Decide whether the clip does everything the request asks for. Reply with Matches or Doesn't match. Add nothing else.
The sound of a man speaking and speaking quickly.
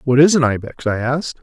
Matches